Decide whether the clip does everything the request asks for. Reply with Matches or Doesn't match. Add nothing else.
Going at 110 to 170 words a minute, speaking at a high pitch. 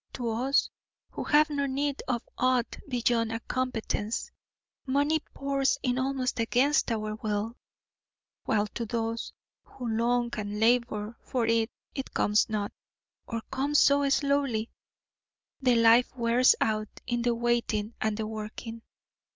Matches